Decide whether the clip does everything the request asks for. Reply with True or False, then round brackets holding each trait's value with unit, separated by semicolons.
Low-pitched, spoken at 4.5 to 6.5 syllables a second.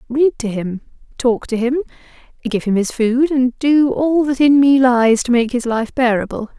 False (250 Hz; 4.7 syllables/s)